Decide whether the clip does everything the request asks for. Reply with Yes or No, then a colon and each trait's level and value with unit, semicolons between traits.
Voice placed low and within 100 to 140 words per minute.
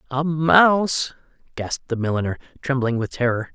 Yes: low, 130 Hz; slow, 135 wpm